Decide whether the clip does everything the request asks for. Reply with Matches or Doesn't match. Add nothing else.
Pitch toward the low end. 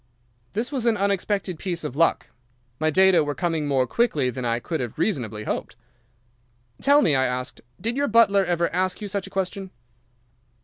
Doesn't match